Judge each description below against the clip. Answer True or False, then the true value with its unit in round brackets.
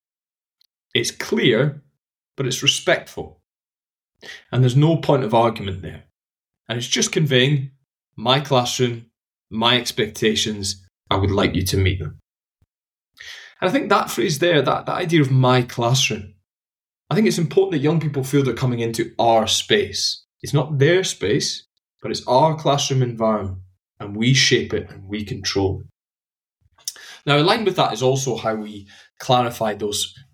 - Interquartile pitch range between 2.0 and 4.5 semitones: False (5.2 semitones)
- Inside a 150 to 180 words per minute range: True (155 wpm)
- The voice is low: True (125 Hz)